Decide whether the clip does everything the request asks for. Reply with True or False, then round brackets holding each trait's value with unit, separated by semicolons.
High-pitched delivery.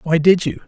False (165 Hz)